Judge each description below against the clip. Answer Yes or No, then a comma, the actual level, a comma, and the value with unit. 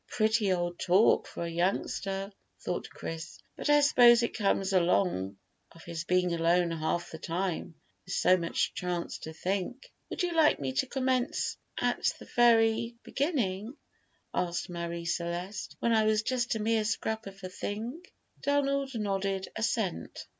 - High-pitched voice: Yes, high, 195 Hz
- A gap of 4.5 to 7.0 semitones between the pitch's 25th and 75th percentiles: Yes, average, 5.1 semitones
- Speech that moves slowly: No, average, 155 wpm